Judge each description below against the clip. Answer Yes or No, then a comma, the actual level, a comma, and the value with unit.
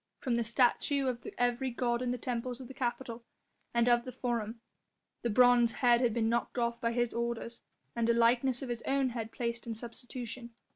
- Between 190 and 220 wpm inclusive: Yes, average, 200 wpm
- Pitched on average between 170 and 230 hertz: No, high, 240 Hz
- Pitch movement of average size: No, narrow, 1.0 semitones